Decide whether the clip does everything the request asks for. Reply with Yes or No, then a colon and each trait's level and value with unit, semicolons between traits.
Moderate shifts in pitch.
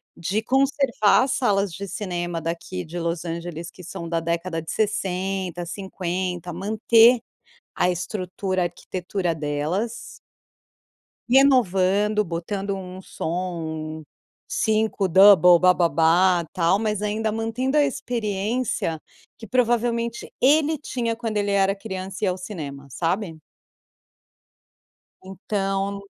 Yes: average, 4.0 semitones